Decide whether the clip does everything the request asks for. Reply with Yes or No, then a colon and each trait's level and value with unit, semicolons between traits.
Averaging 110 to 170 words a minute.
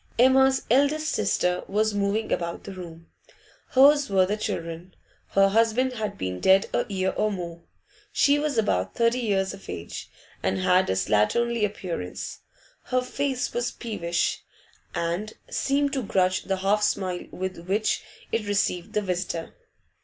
Yes: average, 150 wpm